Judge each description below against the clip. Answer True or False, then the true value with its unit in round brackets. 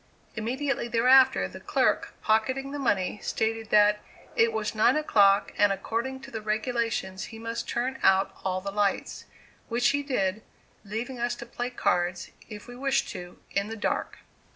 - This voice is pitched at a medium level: False (225 Hz)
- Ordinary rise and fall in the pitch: True (3.2 semitones)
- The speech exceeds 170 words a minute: False (165 wpm)